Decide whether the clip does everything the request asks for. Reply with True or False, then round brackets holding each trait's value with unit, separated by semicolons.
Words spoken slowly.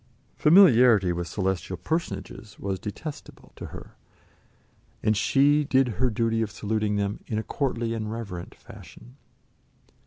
True (130 wpm)